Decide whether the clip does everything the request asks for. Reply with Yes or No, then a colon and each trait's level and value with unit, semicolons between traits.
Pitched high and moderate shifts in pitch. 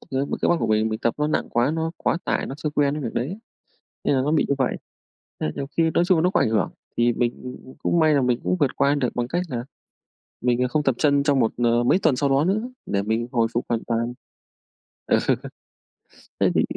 No: low, 135 Hz; average, 4.3 semitones